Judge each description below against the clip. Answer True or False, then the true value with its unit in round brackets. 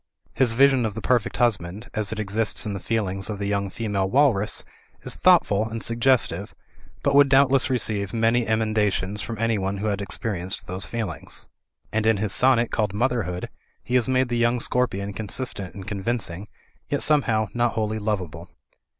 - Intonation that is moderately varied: True (3.2 semitones)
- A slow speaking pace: False (175 wpm)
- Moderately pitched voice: False (110 Hz)